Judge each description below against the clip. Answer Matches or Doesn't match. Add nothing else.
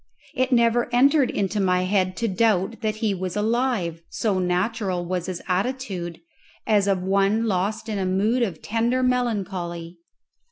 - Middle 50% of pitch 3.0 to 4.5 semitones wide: Matches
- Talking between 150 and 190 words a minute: Matches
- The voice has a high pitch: Matches